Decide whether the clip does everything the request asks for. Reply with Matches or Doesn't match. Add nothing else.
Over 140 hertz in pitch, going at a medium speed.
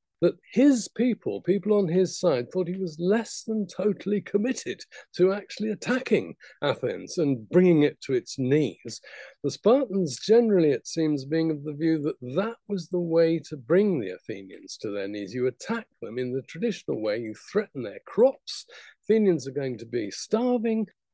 Matches